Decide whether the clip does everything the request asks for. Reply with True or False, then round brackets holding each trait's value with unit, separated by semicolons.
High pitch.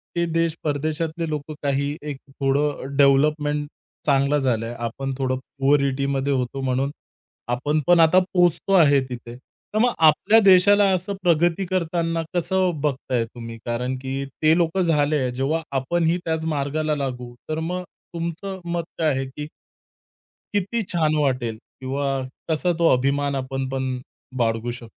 False (145 Hz)